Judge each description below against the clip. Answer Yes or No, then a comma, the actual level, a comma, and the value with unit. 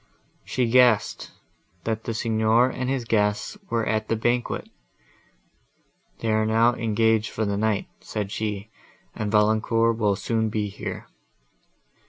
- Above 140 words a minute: No, slow, 135 wpm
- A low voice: Yes, low, 110 Hz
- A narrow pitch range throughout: Yes, narrow, 1.3 semitones